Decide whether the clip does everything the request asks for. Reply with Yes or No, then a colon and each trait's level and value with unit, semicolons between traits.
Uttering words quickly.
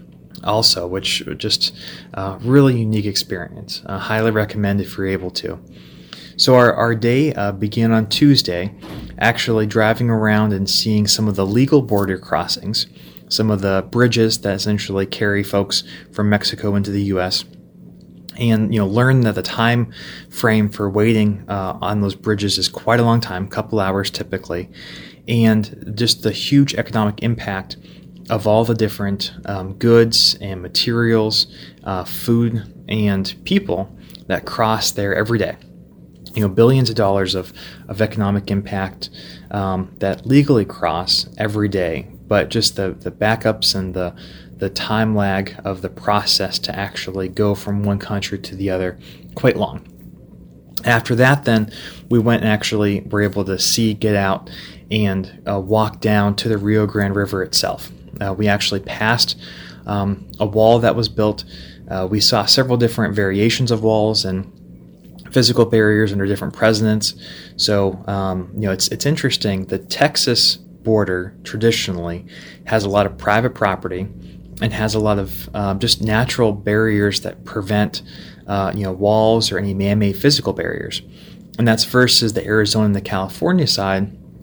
No: average, 160 wpm